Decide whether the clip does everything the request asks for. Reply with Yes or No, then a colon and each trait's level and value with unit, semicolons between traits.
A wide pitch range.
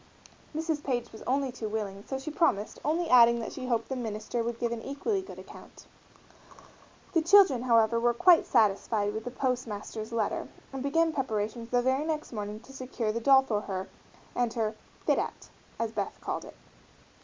No: average, 3.7 semitones